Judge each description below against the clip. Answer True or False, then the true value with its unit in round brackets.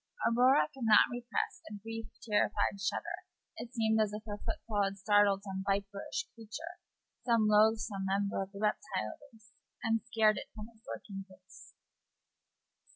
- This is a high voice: True (210 Hz)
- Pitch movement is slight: True (2.2 semitones)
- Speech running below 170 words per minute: True (155 wpm)